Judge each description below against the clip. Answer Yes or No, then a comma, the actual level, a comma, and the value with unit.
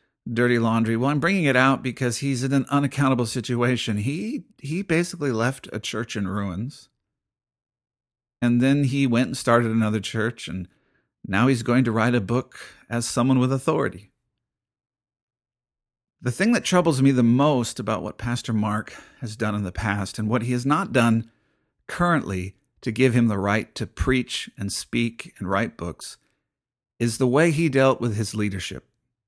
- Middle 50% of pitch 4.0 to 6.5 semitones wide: No, average, 3.4 semitones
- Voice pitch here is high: No, low, 120 Hz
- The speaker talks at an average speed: Yes, average, 170 wpm